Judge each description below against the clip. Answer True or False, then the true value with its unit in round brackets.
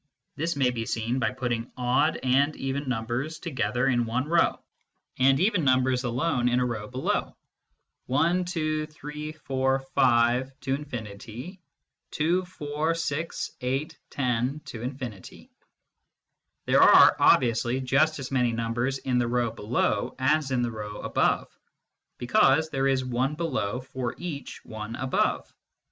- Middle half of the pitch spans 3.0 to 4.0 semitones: True (3.6 semitones)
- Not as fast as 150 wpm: True (140 wpm)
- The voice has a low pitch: True (130 Hz)